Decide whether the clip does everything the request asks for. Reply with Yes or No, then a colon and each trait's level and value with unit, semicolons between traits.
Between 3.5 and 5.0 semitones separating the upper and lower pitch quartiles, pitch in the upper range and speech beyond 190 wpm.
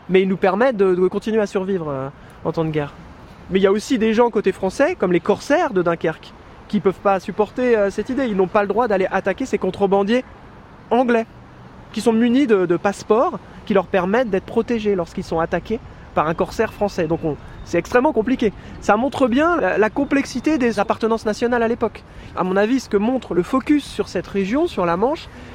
Yes: average, 4.0 semitones; high, 205 Hz; fast, 220 wpm